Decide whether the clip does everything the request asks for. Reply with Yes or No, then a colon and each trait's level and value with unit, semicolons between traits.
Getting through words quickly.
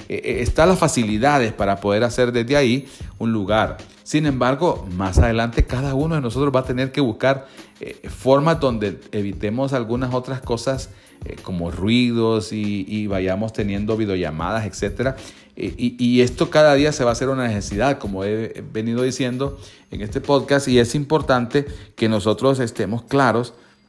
No: average, 165 wpm